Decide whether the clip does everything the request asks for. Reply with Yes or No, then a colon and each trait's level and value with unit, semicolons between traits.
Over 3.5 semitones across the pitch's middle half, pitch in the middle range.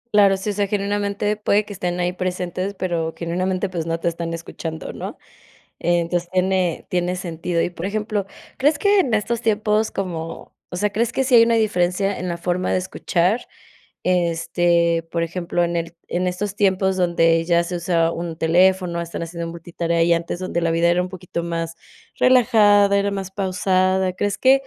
No: average, 3.0 semitones; medium, 180 Hz